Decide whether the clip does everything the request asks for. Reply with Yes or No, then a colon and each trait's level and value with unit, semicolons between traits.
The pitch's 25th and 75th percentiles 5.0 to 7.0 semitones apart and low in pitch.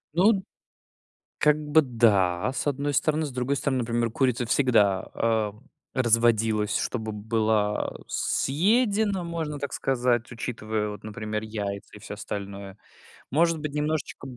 Yes: wide, 5.5 semitones; low, 120 Hz